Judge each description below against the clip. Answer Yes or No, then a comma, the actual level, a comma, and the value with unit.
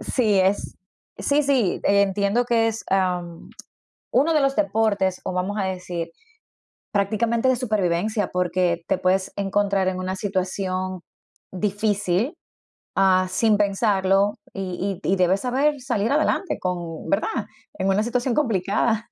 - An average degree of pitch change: Yes, average, 3.4 semitones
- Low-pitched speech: No, high, 200 Hz